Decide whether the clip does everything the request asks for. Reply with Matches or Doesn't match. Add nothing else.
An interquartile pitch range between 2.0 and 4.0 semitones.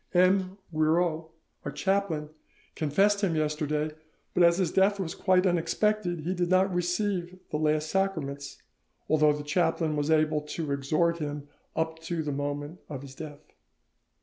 Matches